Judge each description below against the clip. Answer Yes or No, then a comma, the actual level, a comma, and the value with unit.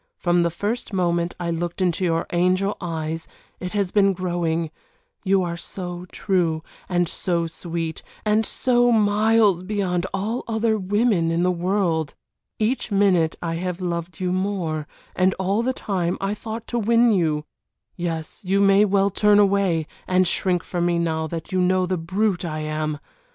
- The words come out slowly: No, average, 165 wpm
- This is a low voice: No, medium, 180 Hz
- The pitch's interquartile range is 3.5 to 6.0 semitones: No, average, 3.0 semitones